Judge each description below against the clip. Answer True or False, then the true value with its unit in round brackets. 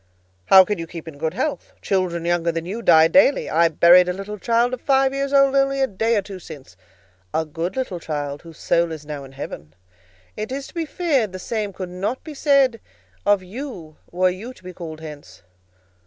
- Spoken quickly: True (210 wpm)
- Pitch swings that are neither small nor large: False (7.1 semitones)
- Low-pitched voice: False (185 Hz)